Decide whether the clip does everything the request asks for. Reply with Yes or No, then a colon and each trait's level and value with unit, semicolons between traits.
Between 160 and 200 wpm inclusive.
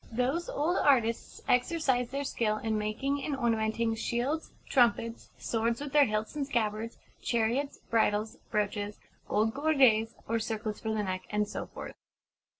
No: average, 150 wpm